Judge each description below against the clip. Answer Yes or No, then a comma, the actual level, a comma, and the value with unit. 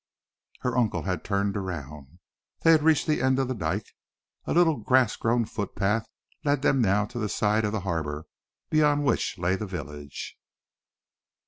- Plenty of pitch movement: Yes, wide, 6.1 semitones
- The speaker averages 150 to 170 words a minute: Yes, average, 165 wpm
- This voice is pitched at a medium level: No, low, 105 Hz